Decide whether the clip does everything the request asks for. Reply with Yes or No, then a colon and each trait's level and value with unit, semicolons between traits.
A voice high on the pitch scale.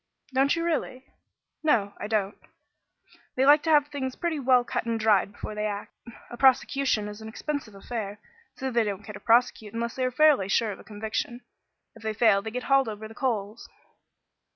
Yes: high, 230 Hz